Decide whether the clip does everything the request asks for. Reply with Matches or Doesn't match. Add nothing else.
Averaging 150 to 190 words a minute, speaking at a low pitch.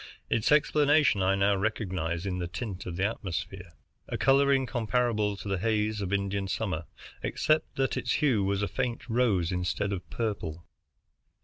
Matches